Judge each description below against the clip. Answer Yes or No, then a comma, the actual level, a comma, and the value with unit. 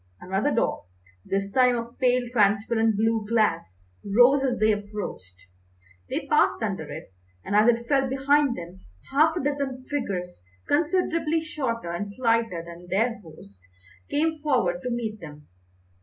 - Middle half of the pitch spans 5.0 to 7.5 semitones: Yes, wide, 5.5 semitones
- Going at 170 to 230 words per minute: No, average, 145 wpm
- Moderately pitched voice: No, high, 230 Hz